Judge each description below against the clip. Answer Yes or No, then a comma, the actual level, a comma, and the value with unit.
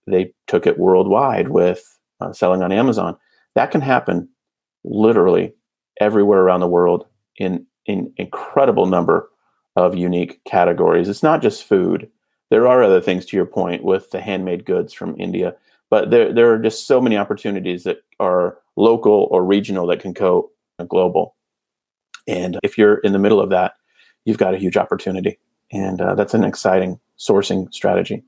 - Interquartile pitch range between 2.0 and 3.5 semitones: Yes, average, 2.8 semitones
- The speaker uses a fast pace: No, average, 170 wpm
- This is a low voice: Yes, very low, 95 Hz